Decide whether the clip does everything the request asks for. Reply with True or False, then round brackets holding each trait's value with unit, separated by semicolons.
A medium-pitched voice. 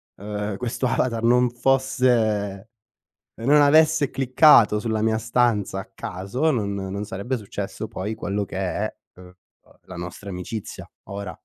False (110 Hz)